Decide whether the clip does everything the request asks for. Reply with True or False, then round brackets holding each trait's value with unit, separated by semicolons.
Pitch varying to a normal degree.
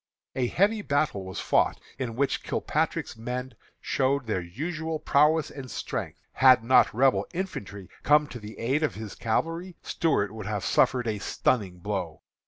False (6.0 semitones)